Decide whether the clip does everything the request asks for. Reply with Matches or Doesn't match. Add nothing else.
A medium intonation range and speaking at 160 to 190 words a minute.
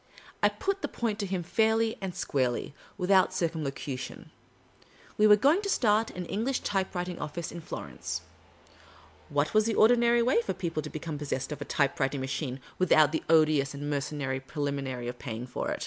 Doesn't match